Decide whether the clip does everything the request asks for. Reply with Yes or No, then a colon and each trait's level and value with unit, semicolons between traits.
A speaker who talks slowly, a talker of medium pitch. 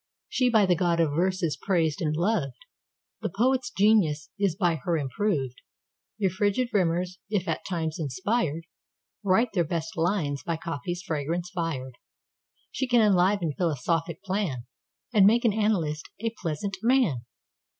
Yes: slow, 130 wpm; medium, 175 Hz